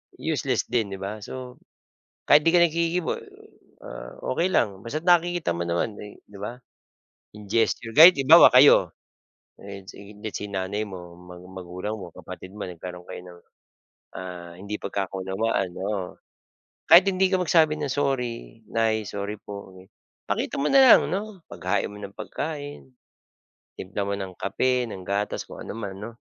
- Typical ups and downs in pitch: No, wide, 6.4 semitones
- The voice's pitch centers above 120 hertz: No, low, 105 Hz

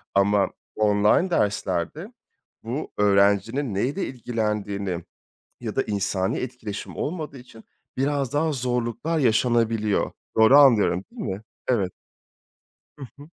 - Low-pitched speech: Yes, low, 115 Hz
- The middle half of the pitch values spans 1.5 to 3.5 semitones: No, average, 4.9 semitones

